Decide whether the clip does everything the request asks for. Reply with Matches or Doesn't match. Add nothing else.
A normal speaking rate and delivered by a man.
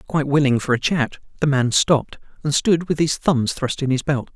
Doesn't match